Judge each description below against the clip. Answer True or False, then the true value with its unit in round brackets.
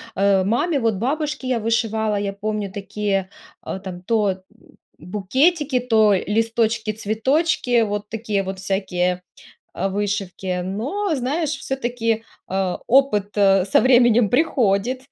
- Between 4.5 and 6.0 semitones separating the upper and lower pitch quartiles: False (4.1 semitones)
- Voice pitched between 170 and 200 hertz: False (215 Hz)